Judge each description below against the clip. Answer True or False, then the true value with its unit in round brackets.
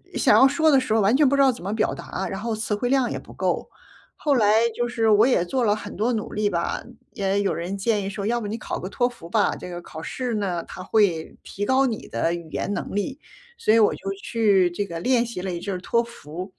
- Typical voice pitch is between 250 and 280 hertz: False (210 Hz)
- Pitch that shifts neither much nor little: True (3.8 semitones)